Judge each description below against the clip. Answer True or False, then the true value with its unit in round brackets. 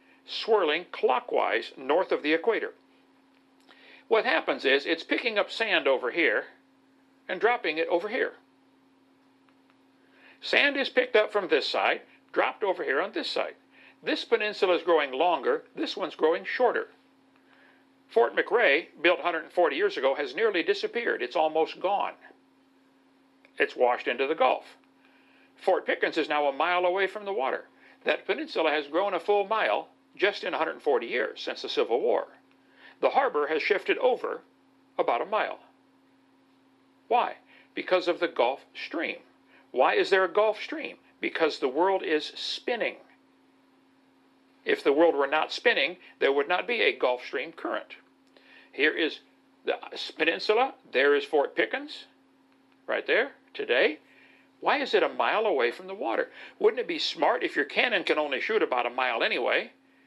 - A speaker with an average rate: True (155 wpm)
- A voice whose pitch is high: True (370 Hz)